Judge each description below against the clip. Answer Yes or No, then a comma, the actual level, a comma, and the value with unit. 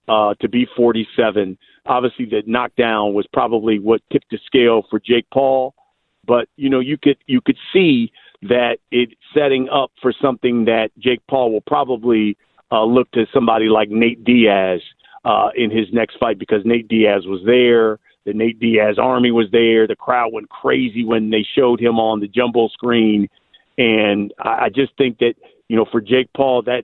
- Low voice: Yes, low, 115 Hz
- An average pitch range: No, narrow, 2.2 semitones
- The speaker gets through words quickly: No, average, 185 wpm